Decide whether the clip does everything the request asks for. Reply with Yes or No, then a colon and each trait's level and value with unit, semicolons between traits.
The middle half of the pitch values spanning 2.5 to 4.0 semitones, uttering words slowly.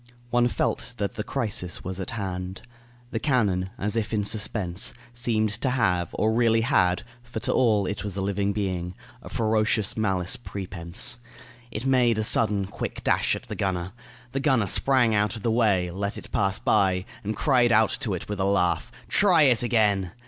No: average, 3.6 semitones; average, 185 wpm